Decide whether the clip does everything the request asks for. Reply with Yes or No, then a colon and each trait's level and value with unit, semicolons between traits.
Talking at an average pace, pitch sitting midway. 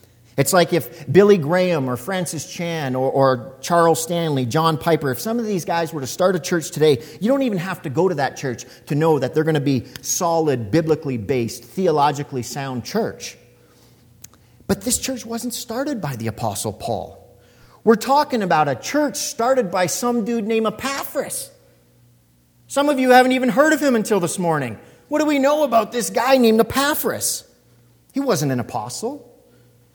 Yes: average, 180 wpm; medium, 165 Hz